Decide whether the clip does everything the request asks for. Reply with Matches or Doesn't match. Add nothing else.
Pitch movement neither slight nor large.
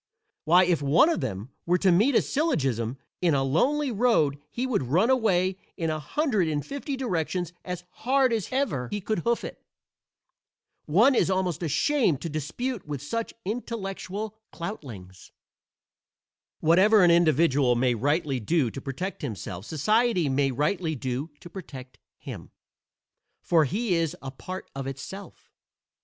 Doesn't match